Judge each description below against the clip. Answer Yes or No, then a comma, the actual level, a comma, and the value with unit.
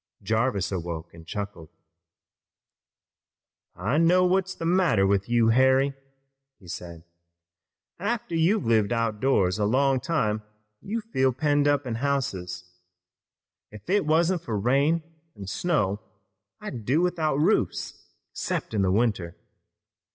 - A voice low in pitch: Yes, low, 125 Hz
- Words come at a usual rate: No, slow, 130 wpm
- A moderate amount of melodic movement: No, wide, 7.7 semitones